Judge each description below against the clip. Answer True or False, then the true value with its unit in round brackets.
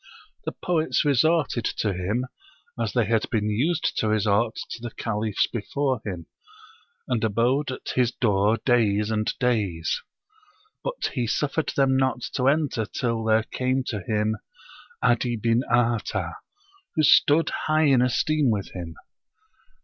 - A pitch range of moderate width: True (3.7 semitones)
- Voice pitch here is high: False (120 Hz)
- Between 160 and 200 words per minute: False (140 wpm)